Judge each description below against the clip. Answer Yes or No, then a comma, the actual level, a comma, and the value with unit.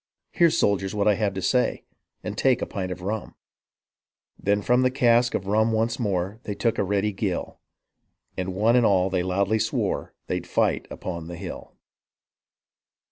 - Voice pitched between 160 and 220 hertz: No, low, 100 Hz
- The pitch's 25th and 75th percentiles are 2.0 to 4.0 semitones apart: Yes, average, 3.3 semitones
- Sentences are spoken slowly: No, average, 180 wpm